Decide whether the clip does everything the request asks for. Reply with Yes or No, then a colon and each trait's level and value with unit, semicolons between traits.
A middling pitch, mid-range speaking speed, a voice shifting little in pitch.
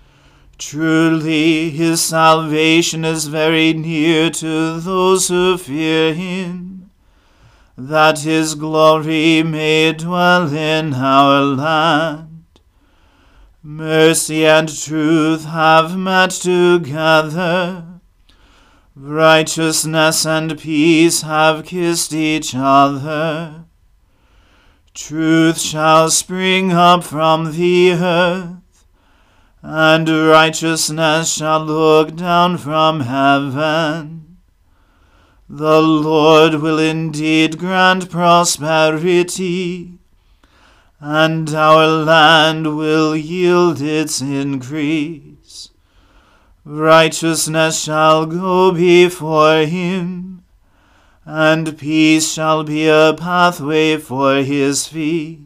No: medium, 160 Hz; slow, 80 wpm; narrow, 1.1 semitones